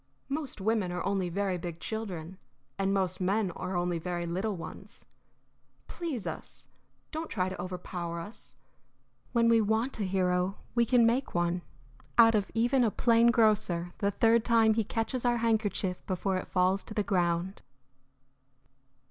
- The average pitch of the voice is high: Yes, high, 200 Hz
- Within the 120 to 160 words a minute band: Yes, average, 155 wpm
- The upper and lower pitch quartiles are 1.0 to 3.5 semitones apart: No, average, 4.0 semitones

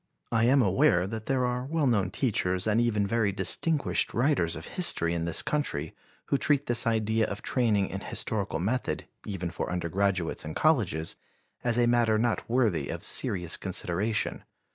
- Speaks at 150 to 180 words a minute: Yes, average, 165 wpm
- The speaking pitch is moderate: No, low, 110 Hz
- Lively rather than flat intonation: No, average, 4.9 semitones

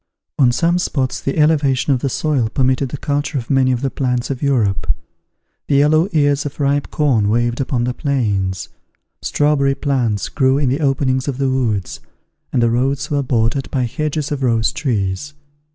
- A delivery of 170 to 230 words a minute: Yes, average, 180 wpm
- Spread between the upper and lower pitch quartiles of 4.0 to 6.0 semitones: No, average, 2.9 semitones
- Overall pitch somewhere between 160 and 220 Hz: No, low, 135 Hz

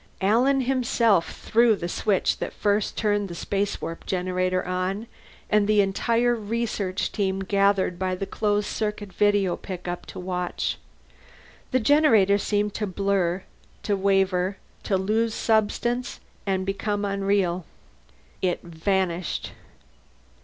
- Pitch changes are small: Yes, narrow, 2.3 semitones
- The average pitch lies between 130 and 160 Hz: No, high, 200 Hz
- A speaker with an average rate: No, slow, 120 wpm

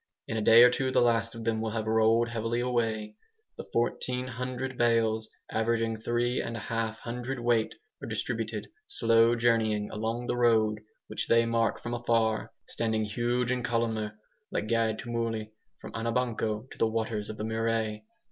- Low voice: Yes, low, 115 Hz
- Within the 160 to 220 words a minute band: Yes, average, 165 wpm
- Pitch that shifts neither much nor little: No, narrow, 1.3 semitones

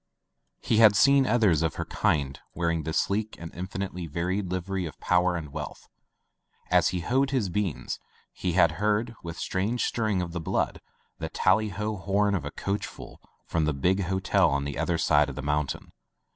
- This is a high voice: No, very low, 90 Hz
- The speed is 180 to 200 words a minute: Yes, average, 185 wpm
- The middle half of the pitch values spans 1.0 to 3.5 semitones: No, average, 4.0 semitones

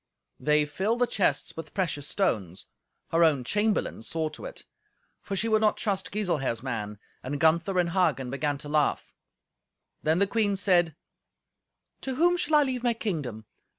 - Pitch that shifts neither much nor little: No, wide, 6.4 semitones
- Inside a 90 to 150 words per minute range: No, average, 165 wpm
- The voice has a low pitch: No, medium, 170 Hz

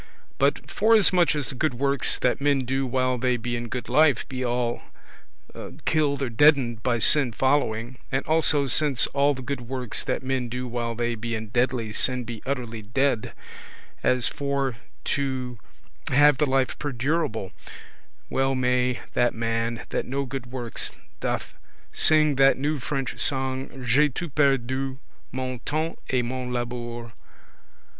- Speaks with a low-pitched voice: Yes, low, 130 Hz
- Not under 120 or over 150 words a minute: No, average, 160 wpm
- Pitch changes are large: No, narrow, 2.6 semitones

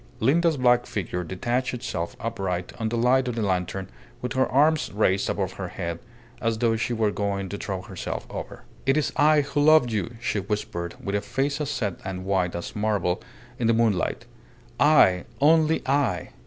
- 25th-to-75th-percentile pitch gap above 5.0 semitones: Yes, wide, 5.5 semitones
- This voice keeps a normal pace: Yes, average, 185 wpm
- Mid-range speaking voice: No, low, 110 Hz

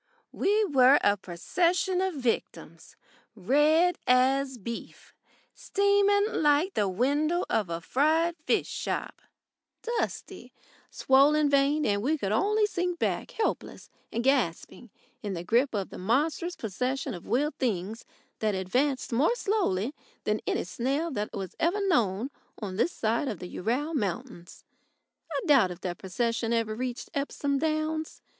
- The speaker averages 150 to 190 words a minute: No, average, 140 wpm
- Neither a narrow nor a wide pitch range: No, wide, 6.7 semitones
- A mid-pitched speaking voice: No, very high, 265 Hz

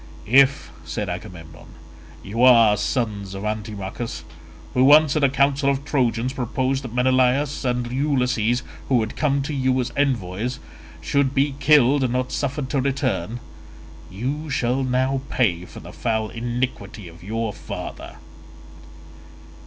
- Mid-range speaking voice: No, low, 125 Hz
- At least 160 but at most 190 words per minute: No, average, 140 wpm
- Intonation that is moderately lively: Yes, average, 3.8 semitones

